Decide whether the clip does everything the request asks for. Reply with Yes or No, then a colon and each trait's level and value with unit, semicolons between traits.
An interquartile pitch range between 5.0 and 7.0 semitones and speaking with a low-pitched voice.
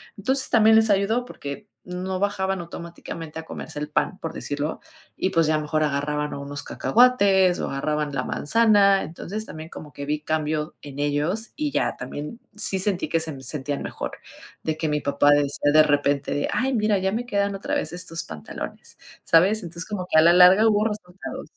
No: average, 5.3 semitones; medium, 170 Hz